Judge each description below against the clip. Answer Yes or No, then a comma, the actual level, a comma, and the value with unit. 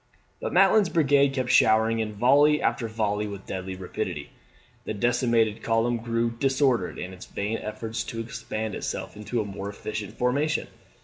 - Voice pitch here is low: Yes, low, 115 Hz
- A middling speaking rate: Yes, average, 160 wpm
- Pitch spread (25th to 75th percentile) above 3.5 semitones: No, average, 2.9 semitones